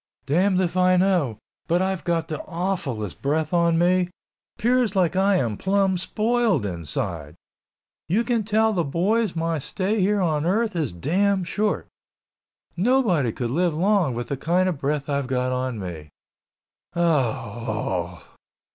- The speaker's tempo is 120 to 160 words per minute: Yes, average, 150 wpm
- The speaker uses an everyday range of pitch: No, wide, 6.5 semitones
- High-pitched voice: No, medium, 170 Hz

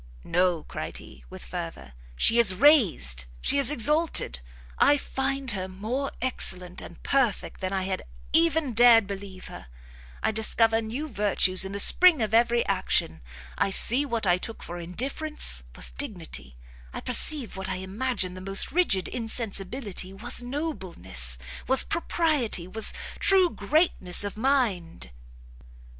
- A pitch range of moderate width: No, wide, 6.3 semitones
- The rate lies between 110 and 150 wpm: Yes, average, 145 wpm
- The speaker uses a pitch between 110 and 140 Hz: No, high, 215 Hz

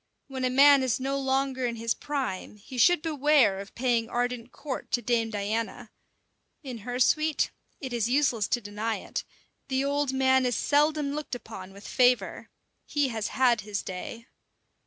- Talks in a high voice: Yes, very high, 250 Hz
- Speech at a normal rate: Yes, average, 170 wpm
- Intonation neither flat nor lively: Yes, average, 3.3 semitones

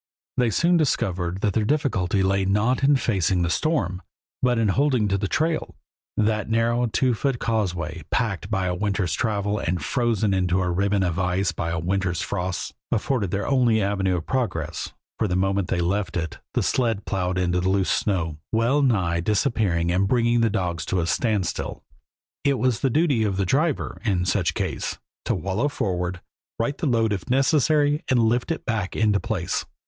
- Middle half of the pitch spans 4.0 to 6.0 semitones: Yes, average, 4.6 semitones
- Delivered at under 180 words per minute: No, average, 185 wpm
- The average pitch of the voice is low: Yes, low, 100 Hz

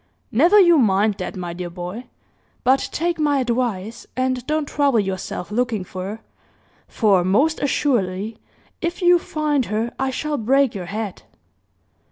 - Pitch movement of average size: No, wide, 6.7 semitones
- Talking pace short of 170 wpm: Yes, average, 150 wpm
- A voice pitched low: No, high, 235 Hz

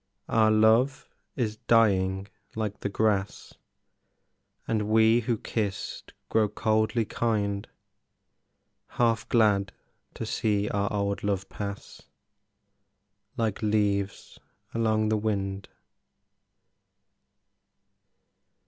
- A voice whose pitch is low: Yes, low, 105 Hz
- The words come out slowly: Yes, slow, 85 wpm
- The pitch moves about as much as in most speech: No, narrow, 1.8 semitones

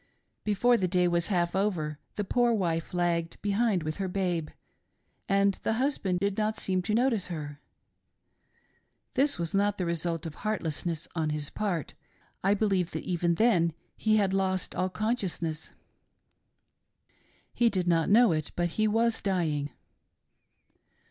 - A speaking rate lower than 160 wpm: Yes, average, 150 wpm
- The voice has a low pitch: No, medium, 185 Hz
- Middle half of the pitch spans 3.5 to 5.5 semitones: Yes, average, 4.0 semitones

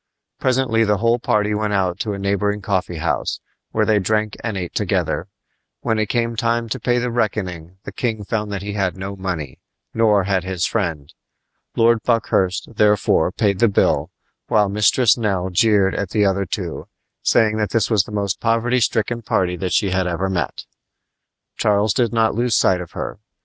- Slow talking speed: No, average, 185 wpm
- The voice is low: Yes, low, 105 Hz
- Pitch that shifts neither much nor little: Yes, average, 3.1 semitones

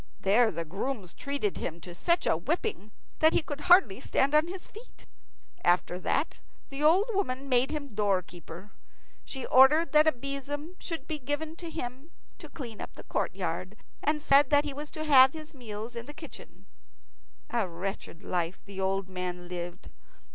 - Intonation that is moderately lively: No, wide, 7.7 semitones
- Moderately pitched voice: No, very high, 265 Hz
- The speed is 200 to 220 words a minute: No, average, 170 wpm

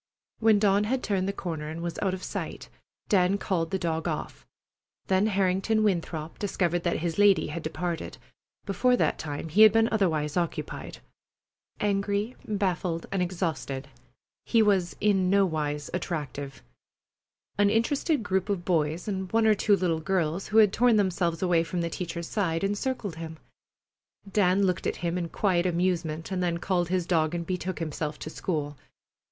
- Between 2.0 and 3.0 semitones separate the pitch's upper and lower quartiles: No, average, 3.4 semitones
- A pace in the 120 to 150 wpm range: No, average, 165 wpm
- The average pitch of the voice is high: No, medium, 180 Hz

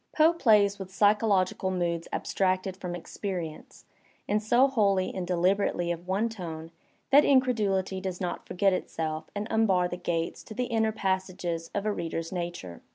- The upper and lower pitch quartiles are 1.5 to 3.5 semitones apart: Yes, average, 3.2 semitones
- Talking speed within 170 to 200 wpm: No, average, 160 wpm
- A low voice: No, high, 190 Hz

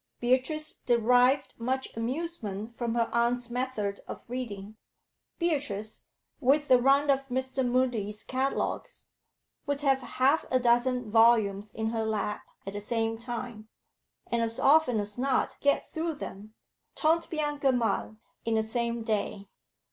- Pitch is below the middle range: No, high, 240 Hz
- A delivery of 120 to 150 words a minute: Yes, average, 140 wpm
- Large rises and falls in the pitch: No, average, 3.2 semitones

